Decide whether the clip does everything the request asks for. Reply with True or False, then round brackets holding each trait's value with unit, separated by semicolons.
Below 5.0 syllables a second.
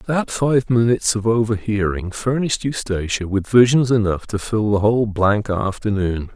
True (4.8 syllables/s)